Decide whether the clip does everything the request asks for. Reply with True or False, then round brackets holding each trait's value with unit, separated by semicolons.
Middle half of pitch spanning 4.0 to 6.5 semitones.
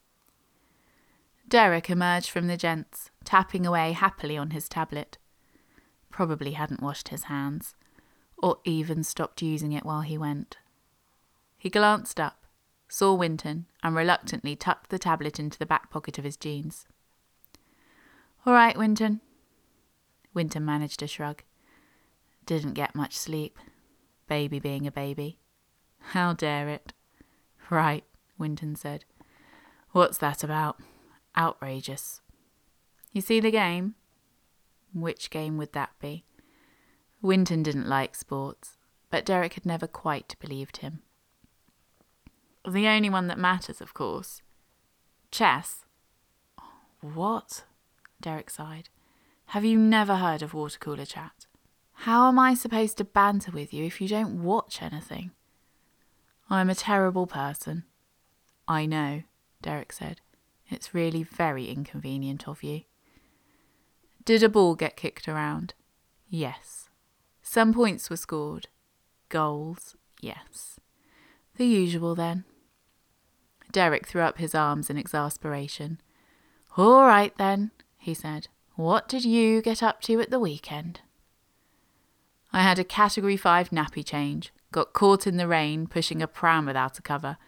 True (4.5 semitones)